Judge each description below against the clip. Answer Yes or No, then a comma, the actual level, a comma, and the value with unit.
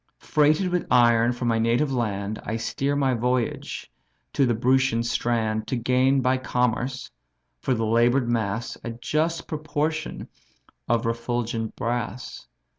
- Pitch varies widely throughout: No, narrow, 2.5 semitones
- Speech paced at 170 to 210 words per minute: No, slow, 135 wpm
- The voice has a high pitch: No, low, 120 Hz